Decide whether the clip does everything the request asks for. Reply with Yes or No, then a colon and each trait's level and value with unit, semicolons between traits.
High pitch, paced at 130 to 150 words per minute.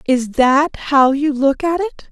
No: very high, 285 Hz; average, 200 wpm